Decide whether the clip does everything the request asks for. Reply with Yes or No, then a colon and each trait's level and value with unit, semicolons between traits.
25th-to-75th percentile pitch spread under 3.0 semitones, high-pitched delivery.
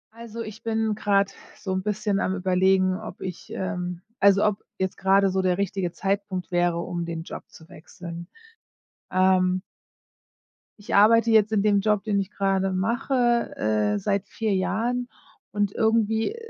Yes: narrow, 2.5 semitones; high, 195 Hz